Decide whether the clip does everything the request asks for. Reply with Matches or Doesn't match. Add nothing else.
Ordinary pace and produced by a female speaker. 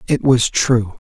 Doesn't match